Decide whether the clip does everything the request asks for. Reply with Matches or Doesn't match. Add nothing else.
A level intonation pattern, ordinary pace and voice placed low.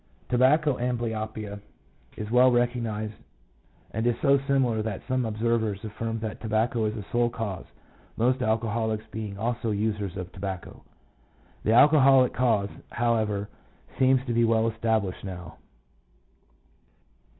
Doesn't match